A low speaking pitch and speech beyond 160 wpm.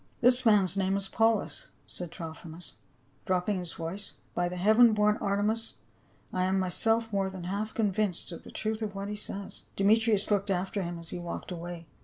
No: high, 195 Hz; average, 195 wpm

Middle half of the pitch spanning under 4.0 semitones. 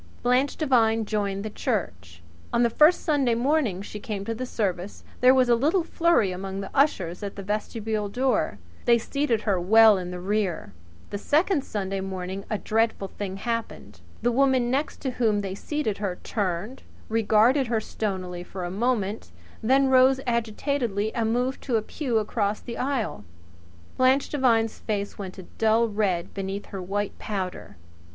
No: average, 4.3 semitones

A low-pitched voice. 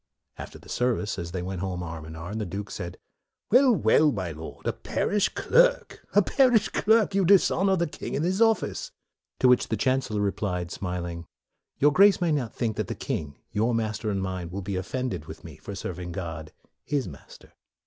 Yes: low, 105 Hz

